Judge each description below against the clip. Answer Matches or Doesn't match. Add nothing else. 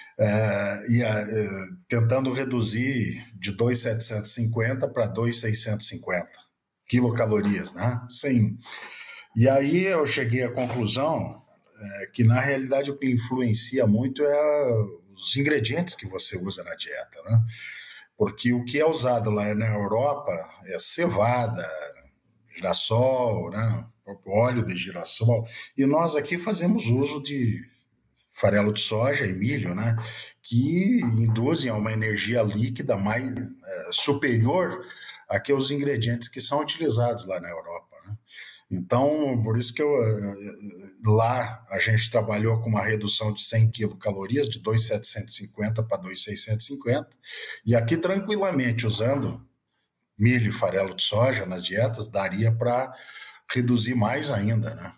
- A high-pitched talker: Doesn't match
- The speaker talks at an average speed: Matches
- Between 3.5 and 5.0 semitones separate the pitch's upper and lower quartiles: Doesn't match